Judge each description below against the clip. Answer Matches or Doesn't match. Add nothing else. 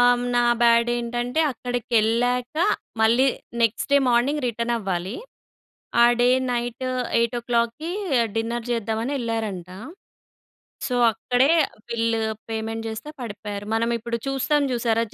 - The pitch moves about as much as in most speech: Doesn't match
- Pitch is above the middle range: Matches